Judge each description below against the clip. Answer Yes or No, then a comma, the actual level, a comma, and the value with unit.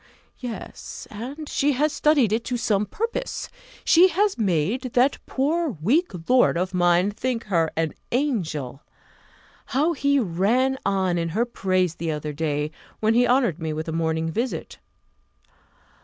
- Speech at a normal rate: Yes, average, 150 wpm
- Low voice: No, high, 215 Hz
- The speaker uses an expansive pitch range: Yes, wide, 8.0 semitones